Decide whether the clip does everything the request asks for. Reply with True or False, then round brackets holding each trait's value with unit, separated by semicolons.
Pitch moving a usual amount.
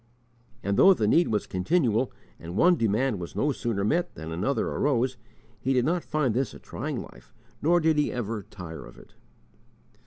False (7.1 semitones)